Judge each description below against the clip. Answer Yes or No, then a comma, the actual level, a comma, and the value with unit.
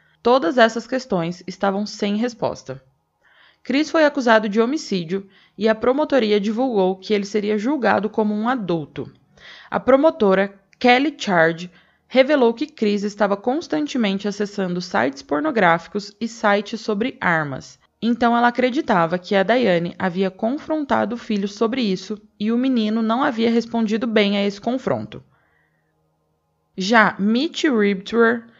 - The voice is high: Yes, high, 215 Hz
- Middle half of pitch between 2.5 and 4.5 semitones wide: Yes, average, 3.8 semitones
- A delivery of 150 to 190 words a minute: No, average, 130 wpm